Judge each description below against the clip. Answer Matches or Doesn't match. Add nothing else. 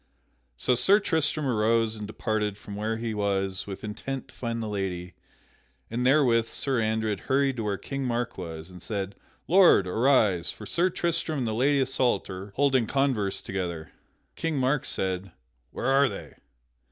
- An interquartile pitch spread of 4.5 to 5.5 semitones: Matches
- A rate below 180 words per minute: Matches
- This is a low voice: Matches